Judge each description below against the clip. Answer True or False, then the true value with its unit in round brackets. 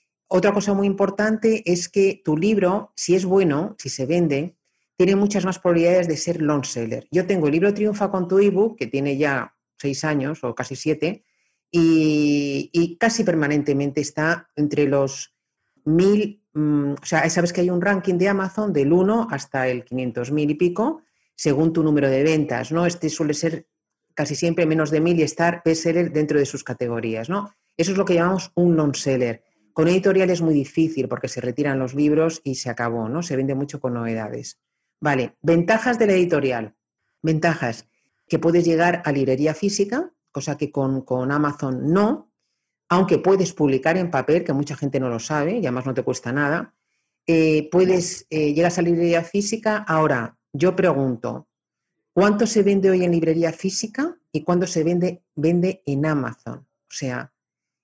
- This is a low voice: False (160 Hz)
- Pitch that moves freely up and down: False (4.5 semitones)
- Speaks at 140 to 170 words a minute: False (180 wpm)